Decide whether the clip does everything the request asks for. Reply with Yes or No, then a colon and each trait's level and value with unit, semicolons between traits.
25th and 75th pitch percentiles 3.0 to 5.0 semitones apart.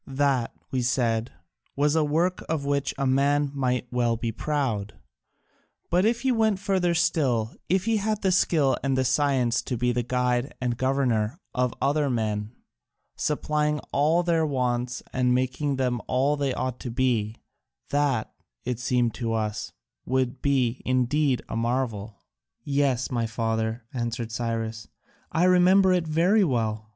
Yes: average, 4.0 semitones